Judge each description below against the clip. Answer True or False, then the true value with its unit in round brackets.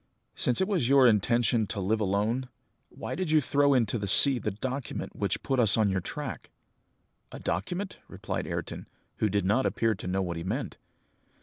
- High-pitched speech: False (115 Hz)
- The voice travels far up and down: False (5.0 semitones)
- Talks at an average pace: True (190 wpm)